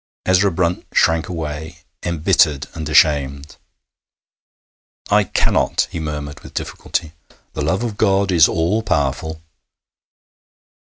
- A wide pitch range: No, average, 3.4 semitones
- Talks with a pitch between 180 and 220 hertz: No, very low, 80 Hz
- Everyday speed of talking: No, slow, 110 wpm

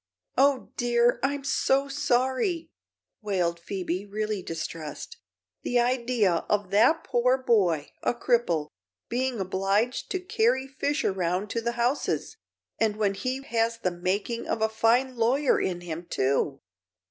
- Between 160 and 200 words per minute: No, slow, 135 wpm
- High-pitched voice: Yes, high, 230 Hz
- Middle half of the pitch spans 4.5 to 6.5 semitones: Yes, average, 5.2 semitones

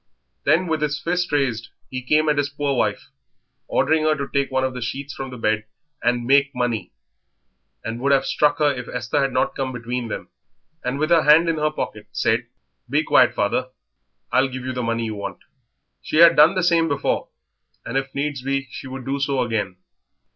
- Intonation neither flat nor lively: Yes, average, 3.3 semitones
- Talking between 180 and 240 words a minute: Yes, fast, 205 wpm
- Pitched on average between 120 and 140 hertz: Yes, low, 135 Hz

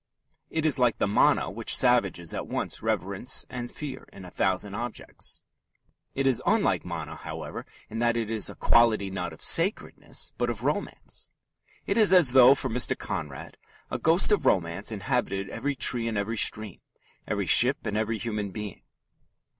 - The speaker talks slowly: No, average, 170 wpm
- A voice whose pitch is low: Yes, low, 115 Hz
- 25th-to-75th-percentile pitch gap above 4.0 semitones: Yes, average, 4.6 semitones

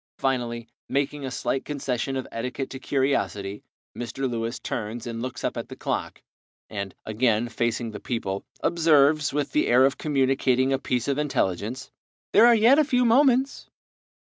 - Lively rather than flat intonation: No, average, 3.6 semitones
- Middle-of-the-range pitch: No, low, 130 Hz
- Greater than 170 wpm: No, average, 165 wpm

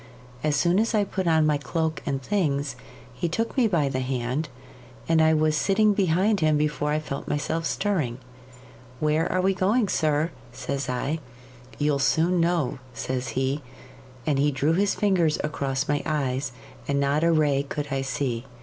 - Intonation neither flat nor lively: Yes, average, 3.7 semitones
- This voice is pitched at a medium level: Yes, medium, 150 Hz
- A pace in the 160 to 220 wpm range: Yes, average, 175 wpm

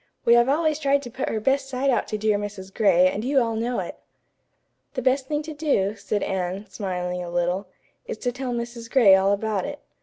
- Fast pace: Yes, fast, 220 wpm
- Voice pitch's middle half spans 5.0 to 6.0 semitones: Yes, wide, 5.4 semitones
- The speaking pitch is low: No, high, 230 Hz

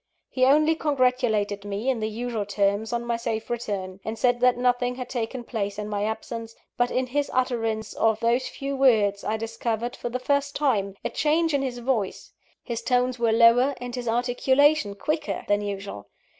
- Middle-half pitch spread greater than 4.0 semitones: No, average, 2.8 semitones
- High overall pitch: Yes, high, 240 Hz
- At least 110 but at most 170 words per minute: No, average, 185 wpm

